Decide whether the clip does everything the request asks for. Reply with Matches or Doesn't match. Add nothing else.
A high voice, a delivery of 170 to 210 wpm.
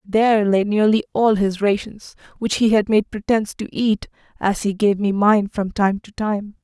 Matches